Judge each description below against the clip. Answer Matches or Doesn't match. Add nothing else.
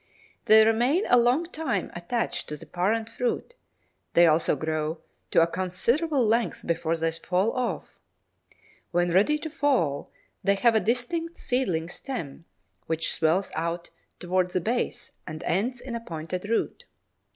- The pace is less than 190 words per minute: Matches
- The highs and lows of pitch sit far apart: Matches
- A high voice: Matches